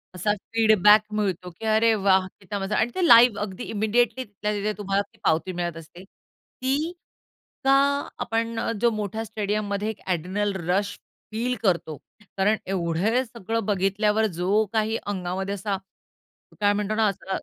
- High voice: Yes, high, 205 Hz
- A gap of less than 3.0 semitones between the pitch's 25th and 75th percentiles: Yes, narrow, 2.5 semitones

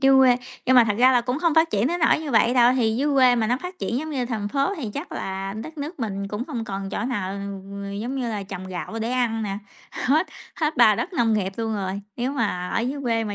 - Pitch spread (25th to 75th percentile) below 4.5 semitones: No, average, 4.9 semitones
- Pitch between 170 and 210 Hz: No, high, 235 Hz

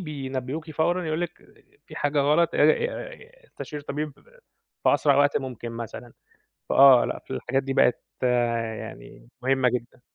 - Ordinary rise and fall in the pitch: Yes, average, 3.7 semitones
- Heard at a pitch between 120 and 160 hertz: Yes, low, 135 Hz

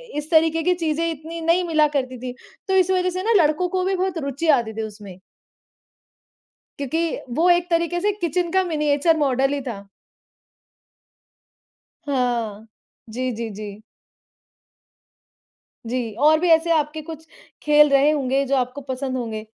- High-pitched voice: Yes, very high, 300 Hz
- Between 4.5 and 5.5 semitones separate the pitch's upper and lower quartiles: Yes, average, 4.8 semitones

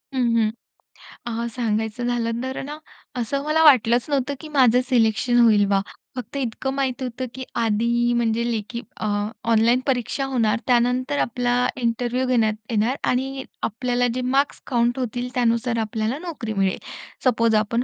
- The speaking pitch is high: Yes, high, 240 Hz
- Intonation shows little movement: Yes, narrow, 2.0 semitones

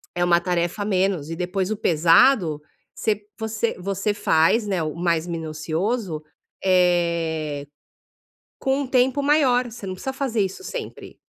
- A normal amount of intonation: Yes, average, 5.0 semitones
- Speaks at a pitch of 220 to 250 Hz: No, medium, 185 Hz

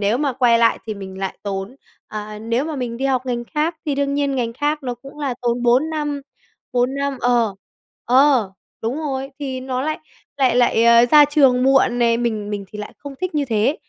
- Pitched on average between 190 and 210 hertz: No, very high, 250 Hz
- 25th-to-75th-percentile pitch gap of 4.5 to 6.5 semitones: No, average, 3.3 semitones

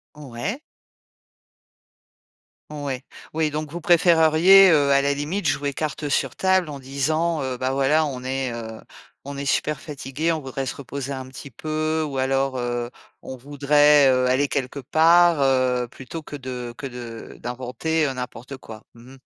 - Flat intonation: No, average, 3.2 semitones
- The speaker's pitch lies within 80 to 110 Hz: No, medium, 140 Hz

